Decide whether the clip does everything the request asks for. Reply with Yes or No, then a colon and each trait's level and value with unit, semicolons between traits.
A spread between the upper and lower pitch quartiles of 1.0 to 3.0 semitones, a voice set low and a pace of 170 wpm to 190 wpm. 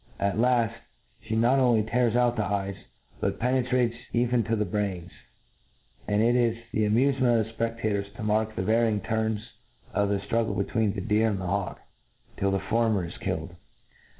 Yes: narrow, 2.5 semitones; low, 110 Hz; average, 180 wpm